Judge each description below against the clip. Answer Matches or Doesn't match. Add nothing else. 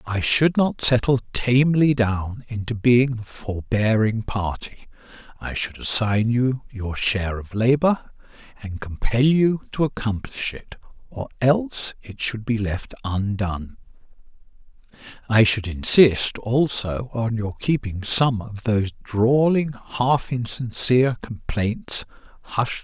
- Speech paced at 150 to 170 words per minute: Doesn't match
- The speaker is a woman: Doesn't match